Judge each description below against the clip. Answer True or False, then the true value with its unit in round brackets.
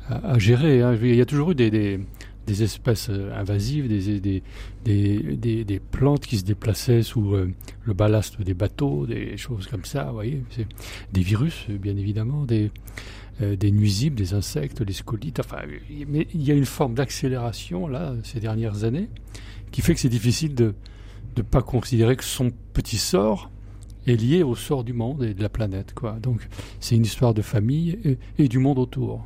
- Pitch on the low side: True (110 Hz)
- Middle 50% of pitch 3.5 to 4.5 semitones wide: True (3.8 semitones)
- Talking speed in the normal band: True (195 wpm)